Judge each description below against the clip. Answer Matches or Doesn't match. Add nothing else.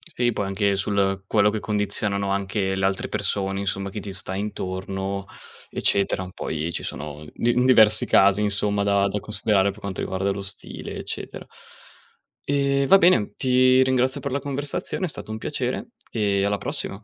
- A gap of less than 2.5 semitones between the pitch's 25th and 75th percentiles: Matches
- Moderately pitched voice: Doesn't match